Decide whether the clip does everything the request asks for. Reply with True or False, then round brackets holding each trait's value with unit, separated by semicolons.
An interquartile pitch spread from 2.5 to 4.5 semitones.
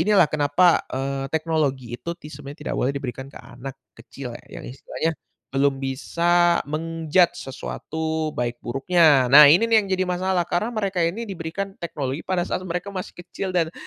False (4.9 semitones)